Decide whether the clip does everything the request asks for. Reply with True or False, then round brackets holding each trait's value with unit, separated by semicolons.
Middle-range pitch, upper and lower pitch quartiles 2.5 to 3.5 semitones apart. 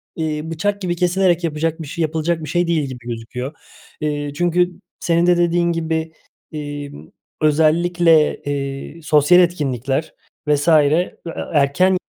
True (160 Hz; 2.9 semitones)